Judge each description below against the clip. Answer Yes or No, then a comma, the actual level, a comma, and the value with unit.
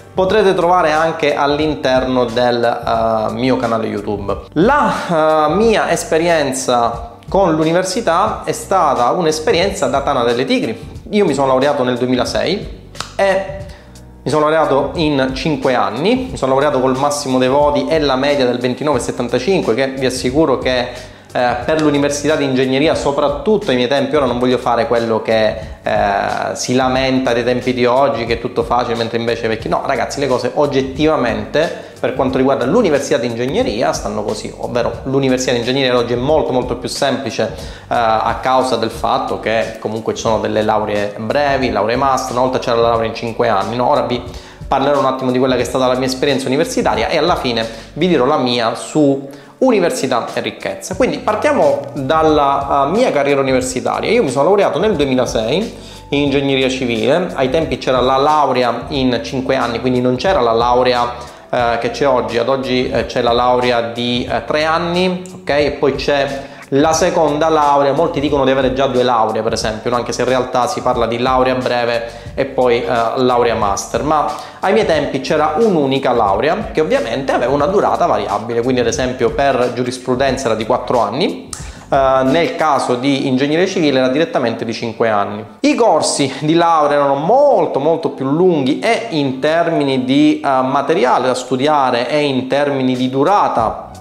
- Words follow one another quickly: Yes, fast, 175 wpm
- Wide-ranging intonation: No, average, 3.6 semitones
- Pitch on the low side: Yes, low, 130 Hz